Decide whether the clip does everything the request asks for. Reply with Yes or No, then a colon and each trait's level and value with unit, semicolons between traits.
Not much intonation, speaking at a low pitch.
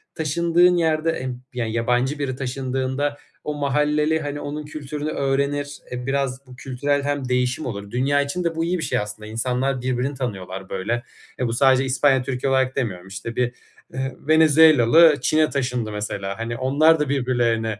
No: average, 3.0 semitones; low, 130 Hz